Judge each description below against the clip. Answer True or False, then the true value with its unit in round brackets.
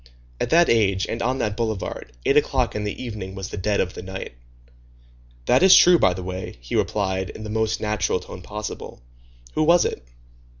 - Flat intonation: False (3.7 semitones)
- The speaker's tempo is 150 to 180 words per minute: False (200 wpm)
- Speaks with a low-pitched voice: True (105 Hz)